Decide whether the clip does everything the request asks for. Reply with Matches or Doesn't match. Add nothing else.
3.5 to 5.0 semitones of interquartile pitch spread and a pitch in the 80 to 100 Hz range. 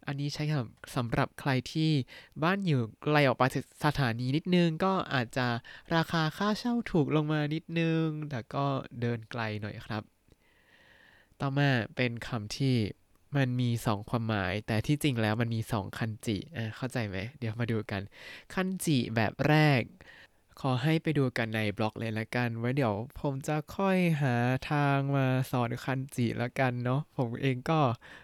Doesn't match